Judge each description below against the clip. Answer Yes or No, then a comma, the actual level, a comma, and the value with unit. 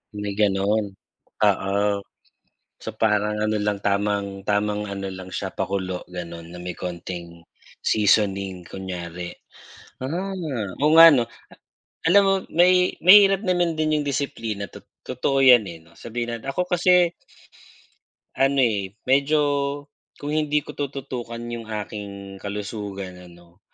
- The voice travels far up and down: Yes, wide, 6.3 semitones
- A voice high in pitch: No, low, 105 Hz